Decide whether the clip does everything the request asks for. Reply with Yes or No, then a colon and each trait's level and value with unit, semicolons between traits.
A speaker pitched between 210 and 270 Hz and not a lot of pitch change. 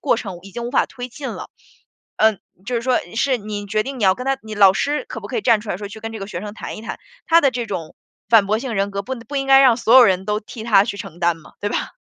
No: high, 220 Hz; average, 3.9 semitones